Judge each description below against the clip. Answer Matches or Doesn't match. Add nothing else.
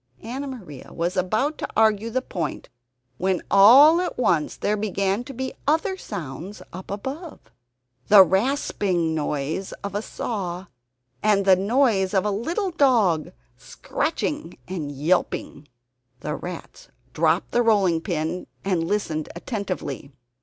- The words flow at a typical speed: Doesn't match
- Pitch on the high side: Matches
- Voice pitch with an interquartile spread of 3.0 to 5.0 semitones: Doesn't match